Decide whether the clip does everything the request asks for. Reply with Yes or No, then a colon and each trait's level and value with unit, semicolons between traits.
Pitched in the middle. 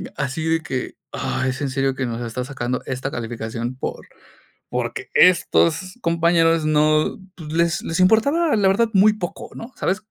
Yes: medium, 160 Hz